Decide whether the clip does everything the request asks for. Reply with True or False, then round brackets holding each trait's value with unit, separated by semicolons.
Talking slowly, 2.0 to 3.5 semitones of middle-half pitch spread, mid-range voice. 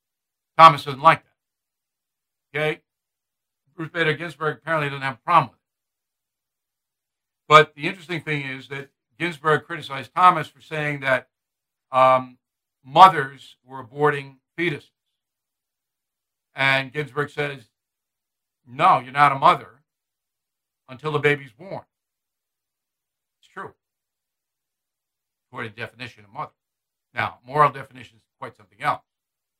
True (120 wpm; 2.8 semitones; 145 Hz)